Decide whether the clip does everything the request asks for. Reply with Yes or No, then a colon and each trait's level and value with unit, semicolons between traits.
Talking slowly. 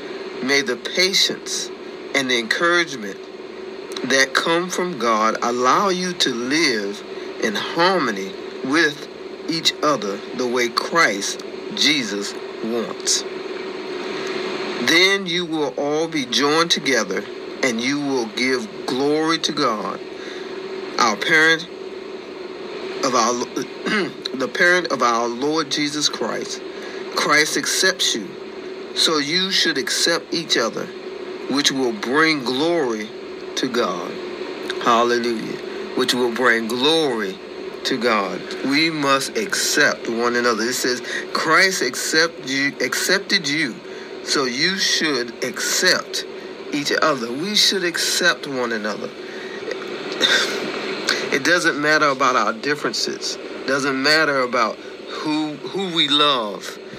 Yes: slow, 115 wpm